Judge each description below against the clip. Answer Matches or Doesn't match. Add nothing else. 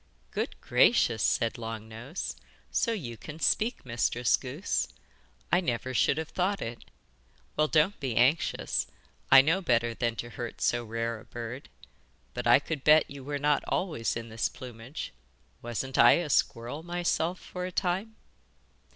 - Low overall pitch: Matches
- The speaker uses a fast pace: Doesn't match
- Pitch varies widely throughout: Matches